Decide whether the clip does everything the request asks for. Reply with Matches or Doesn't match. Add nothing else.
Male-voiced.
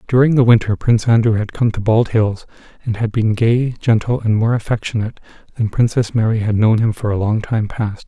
Matches